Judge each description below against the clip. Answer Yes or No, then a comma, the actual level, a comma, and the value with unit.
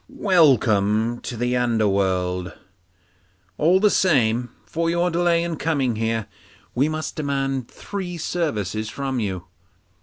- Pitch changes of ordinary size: No, wide, 7.3 semitones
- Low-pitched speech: Yes, low, 130 Hz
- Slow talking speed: Yes, slow, 120 wpm